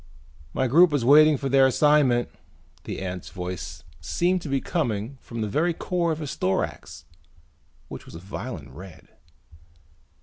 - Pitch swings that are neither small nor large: No, wide, 8.2 semitones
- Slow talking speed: No, average, 155 wpm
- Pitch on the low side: Yes, low, 130 Hz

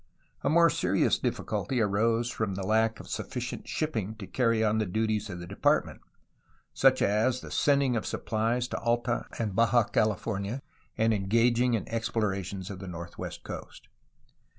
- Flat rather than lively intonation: No, average, 3.1 semitones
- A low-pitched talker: Yes, low, 110 Hz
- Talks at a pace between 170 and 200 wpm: No, average, 155 wpm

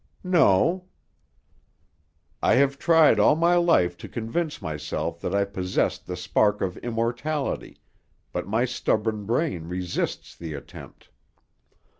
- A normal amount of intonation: No, wide, 8.7 semitones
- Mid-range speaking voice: No, low, 115 Hz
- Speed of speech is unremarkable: No, slow, 120 wpm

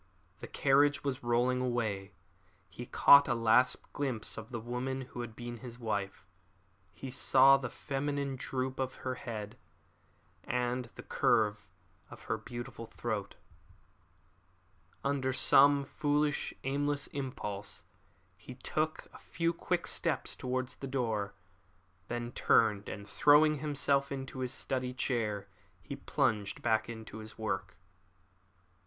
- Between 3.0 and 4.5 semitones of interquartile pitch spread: Yes, average, 3.4 semitones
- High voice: No, low, 125 Hz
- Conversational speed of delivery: No, slow, 130 wpm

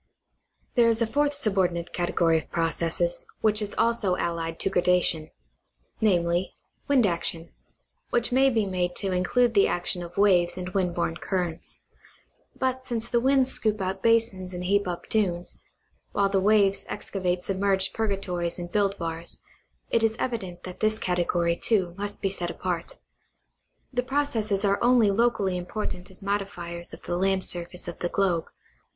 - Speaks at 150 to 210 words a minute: Yes, average, 160 wpm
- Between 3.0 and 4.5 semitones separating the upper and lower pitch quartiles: Yes, average, 3.8 semitones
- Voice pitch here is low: No, high, 195 Hz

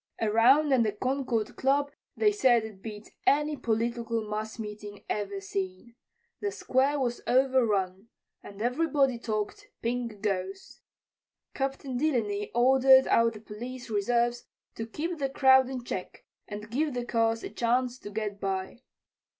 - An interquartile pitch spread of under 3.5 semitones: No, average, 3.9 semitones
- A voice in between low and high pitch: No, high, 235 Hz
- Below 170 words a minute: Yes, average, 140 wpm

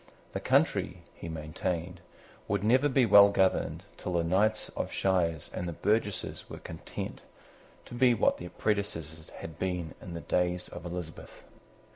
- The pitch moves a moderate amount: Yes, average, 3.5 semitones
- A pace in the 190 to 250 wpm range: No, average, 155 wpm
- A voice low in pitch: Yes, very low, 90 Hz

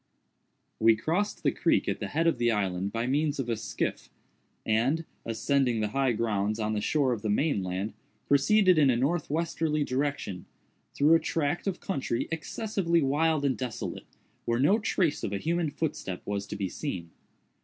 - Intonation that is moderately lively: No, wide, 6.6 semitones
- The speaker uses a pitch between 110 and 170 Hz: Yes, low, 135 Hz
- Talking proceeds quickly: No, average, 175 wpm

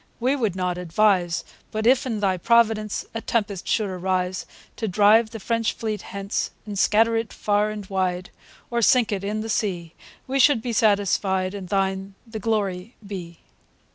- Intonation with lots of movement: No, average, 3.0 semitones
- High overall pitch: Yes, high, 205 Hz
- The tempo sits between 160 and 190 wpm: Yes, average, 170 wpm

